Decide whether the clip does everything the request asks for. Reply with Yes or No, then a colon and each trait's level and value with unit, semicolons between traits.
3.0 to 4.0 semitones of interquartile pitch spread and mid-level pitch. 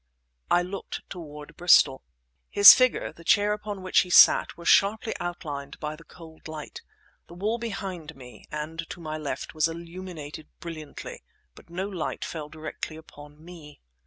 Yes: average, 3.4 semitones; medium, 165 Hz